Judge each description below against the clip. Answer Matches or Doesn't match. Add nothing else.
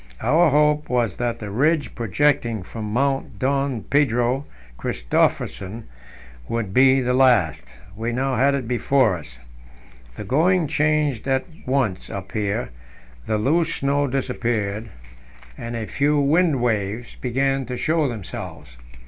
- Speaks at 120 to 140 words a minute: Matches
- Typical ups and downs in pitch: Matches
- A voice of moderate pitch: Doesn't match